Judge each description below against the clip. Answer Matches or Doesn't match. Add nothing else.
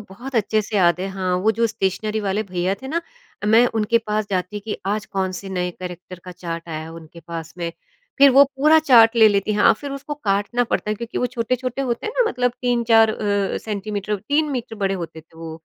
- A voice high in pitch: Matches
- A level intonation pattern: Doesn't match